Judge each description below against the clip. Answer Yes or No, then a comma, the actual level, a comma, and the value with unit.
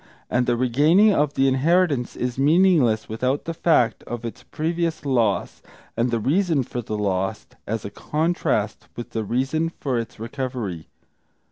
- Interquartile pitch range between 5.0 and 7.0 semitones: Yes, wide, 5.4 semitones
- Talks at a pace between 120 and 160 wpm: Yes, average, 155 wpm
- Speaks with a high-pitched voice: No, low, 130 Hz